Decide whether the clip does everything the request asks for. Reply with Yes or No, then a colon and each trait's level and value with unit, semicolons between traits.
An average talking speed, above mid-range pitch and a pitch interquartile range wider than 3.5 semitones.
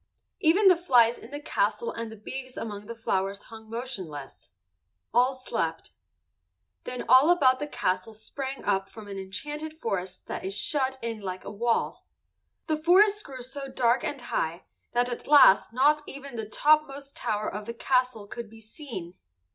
Yes: average, 170 wpm; high, 245 Hz; average, 4.9 semitones